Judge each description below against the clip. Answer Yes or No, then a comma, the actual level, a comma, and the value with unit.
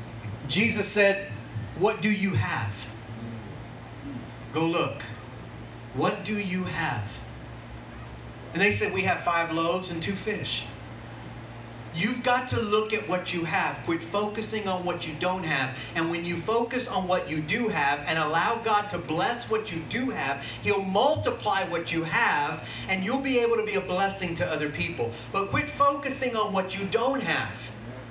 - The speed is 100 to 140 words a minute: No, average, 170 wpm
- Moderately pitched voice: Yes, medium, 170 Hz